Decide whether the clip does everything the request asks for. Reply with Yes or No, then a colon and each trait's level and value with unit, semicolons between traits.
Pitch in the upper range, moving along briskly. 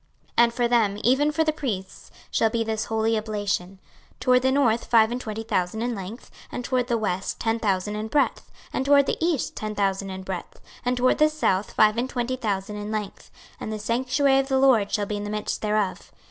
Yes: high, 225 Hz; fast, 220 wpm